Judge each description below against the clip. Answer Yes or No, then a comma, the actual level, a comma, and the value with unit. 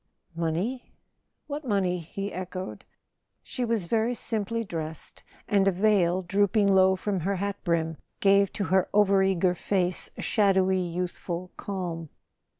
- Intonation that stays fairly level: Yes, narrow, 2.3 semitones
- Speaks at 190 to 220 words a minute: No, average, 140 wpm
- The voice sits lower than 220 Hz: Yes, high, 190 Hz